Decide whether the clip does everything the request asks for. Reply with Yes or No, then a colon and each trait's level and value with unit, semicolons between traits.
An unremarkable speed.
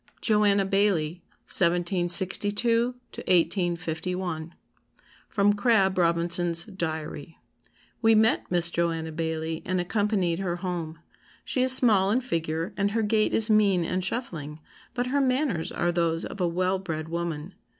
No: slow, 130 wpm